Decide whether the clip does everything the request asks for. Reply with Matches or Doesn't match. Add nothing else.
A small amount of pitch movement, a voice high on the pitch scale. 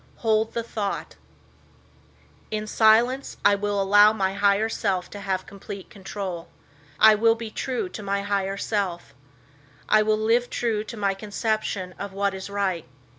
Matches